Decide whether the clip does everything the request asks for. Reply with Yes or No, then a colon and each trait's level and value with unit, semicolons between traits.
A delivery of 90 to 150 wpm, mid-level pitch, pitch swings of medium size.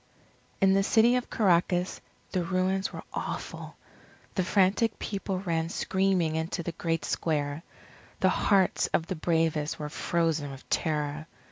Yes: average, 140 wpm; medium, 170 Hz; average, 3.2 semitones